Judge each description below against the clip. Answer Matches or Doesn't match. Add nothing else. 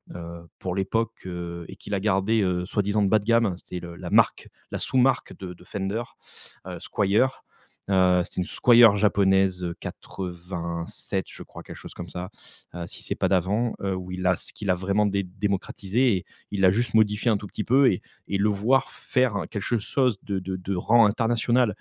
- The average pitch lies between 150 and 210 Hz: Doesn't match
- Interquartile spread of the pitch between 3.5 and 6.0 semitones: Doesn't match